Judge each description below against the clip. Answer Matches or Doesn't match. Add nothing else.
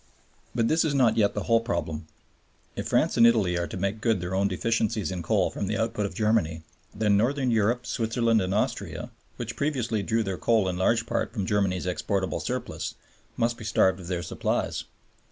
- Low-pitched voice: Matches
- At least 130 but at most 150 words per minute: Doesn't match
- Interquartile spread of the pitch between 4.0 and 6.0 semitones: Doesn't match